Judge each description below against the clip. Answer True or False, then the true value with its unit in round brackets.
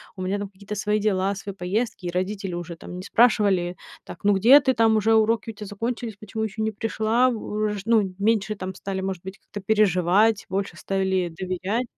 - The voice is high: True (205 Hz)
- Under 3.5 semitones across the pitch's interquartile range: True (2.6 semitones)